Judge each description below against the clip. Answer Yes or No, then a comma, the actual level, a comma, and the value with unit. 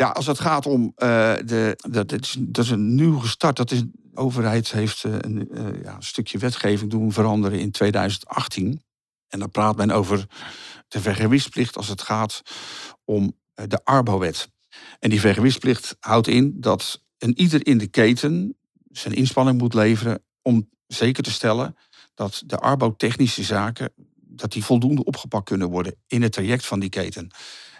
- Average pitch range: Yes, average, 3.4 semitones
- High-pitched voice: No, low, 115 Hz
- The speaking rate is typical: Yes, average, 175 wpm